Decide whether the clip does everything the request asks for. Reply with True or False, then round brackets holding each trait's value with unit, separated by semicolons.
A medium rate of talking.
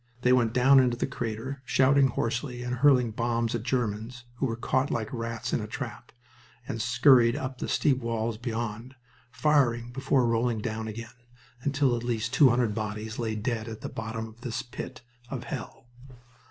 True (180 wpm)